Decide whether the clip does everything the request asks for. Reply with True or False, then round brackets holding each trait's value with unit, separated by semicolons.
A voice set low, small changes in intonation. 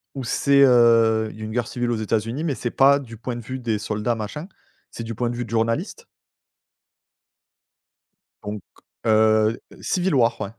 True (115 Hz; 2.3 semitones)